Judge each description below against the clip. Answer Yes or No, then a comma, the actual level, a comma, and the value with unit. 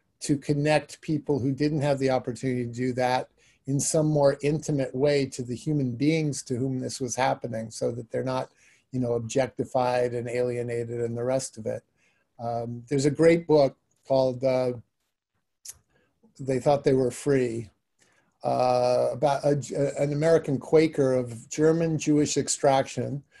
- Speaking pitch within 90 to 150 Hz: Yes, low, 135 Hz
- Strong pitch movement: No, average, 2.8 semitones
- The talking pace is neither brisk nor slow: Yes, average, 160 wpm